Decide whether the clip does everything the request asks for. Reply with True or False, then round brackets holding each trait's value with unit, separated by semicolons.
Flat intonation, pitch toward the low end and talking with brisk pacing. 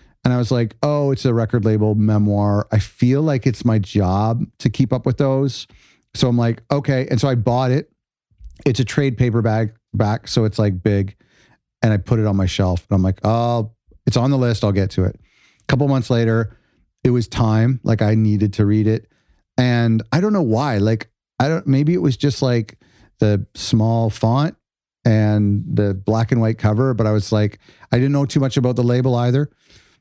False (3.5 semitones; 115 Hz; 210 wpm)